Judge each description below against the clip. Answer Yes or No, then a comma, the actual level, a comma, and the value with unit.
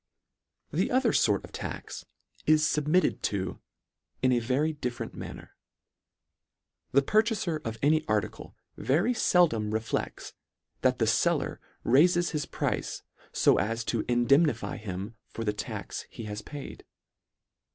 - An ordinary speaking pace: No, slow, 130 wpm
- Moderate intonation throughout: No, wide, 5.9 semitones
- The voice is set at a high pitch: No, low, 135 Hz